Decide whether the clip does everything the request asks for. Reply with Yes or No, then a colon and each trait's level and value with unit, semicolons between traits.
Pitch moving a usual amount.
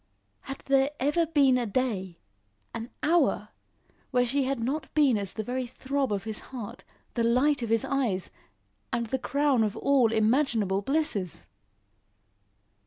Yes: average, 3.9 semitones